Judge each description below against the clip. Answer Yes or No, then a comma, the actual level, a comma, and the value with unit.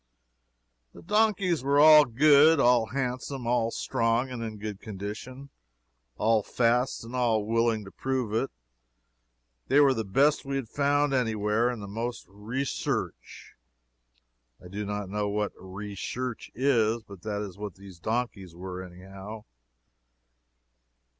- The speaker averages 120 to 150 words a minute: Yes, average, 140 wpm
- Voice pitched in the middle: No, low, 115 Hz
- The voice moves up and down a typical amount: Yes, average, 4.3 semitones